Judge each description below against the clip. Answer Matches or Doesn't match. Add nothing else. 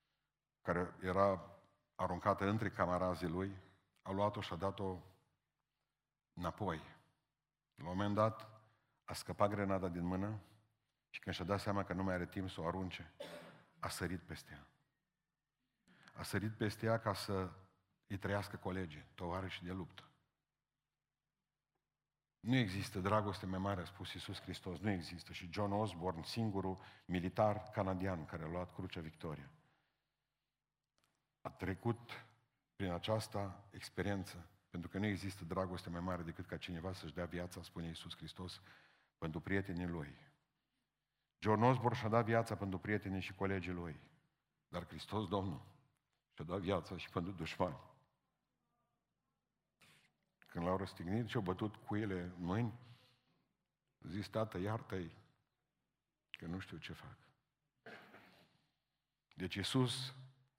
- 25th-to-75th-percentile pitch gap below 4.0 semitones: Matches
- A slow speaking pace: Doesn't match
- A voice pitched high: Doesn't match